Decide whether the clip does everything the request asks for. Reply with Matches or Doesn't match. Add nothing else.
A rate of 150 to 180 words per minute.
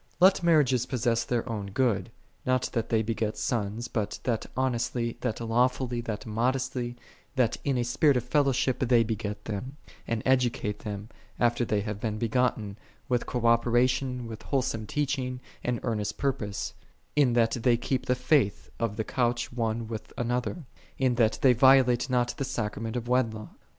Matches